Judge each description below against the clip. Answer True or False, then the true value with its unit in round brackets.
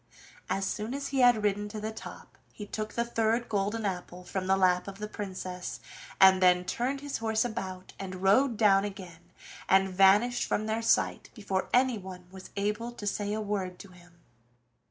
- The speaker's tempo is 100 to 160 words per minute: False (185 wpm)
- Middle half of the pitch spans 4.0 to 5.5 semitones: False (2.8 semitones)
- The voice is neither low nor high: False (205 Hz)